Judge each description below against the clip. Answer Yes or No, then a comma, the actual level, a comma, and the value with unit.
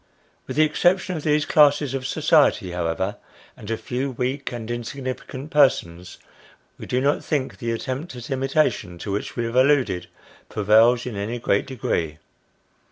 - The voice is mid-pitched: No, low, 125 Hz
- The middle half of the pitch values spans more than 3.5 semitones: Yes, average, 4.7 semitones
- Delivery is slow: No, average, 160 wpm